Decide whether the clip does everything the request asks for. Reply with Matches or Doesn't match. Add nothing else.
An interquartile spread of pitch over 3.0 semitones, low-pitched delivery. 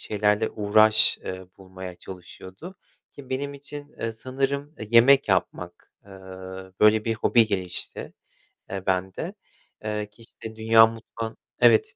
Matches